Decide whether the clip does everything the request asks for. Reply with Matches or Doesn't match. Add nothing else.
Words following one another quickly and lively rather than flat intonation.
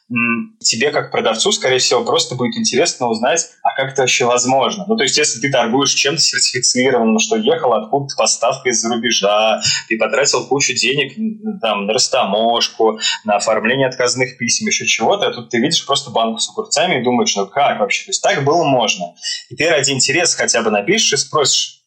Matches